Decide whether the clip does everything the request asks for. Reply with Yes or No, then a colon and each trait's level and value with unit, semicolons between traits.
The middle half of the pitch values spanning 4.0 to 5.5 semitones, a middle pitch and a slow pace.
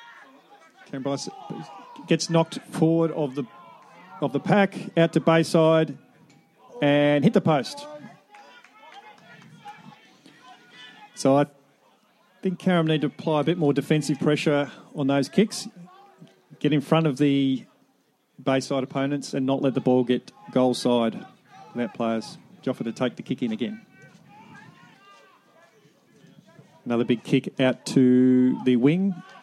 Yes: average, 5.2 semitones; medium, 150 Hz; slow, 130 wpm